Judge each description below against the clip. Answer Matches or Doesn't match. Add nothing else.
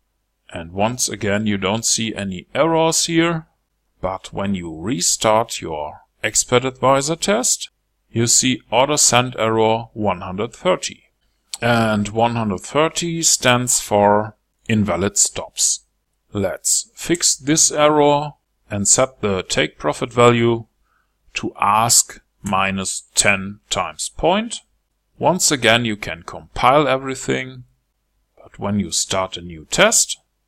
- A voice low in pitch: Matches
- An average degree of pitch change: Matches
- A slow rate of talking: Matches